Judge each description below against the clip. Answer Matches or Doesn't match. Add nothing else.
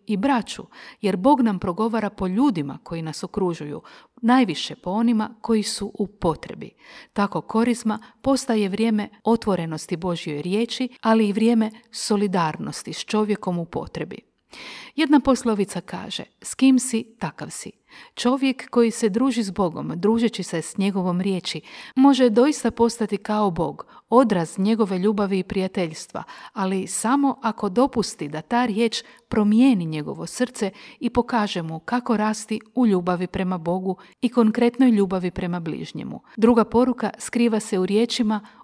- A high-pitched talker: Matches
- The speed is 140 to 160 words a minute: Matches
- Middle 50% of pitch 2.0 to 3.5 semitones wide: Doesn't match